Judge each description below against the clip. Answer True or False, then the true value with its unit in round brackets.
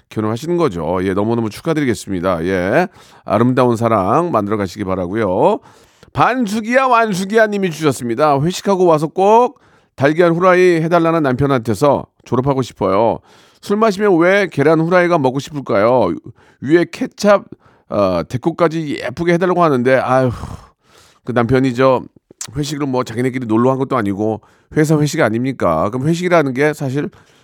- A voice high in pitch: False (140 Hz)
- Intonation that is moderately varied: False (6.2 semitones)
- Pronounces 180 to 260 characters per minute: False (345 characters per minute)